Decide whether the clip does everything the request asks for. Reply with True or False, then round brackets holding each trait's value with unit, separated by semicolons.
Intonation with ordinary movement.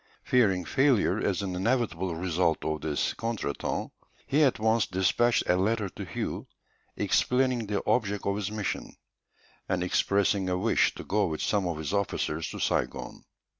True (3.9 semitones)